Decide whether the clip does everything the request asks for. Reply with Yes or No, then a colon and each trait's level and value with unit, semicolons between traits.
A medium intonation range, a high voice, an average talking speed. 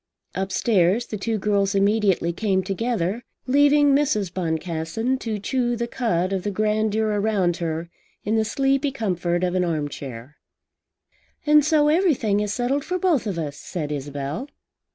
No: wide, 5.7 semitones; high, 210 Hz; average, 155 wpm